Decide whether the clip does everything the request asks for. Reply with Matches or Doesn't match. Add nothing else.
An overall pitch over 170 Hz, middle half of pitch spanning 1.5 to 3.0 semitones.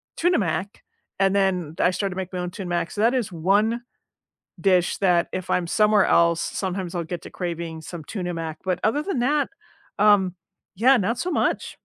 Doesn't match